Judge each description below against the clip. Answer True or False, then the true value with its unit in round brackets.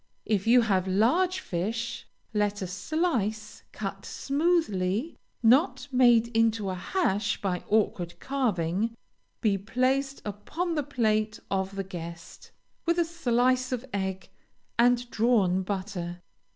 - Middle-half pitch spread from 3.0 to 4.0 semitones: False (4.9 semitones)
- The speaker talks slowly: True (125 wpm)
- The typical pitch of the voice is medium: False (220 Hz)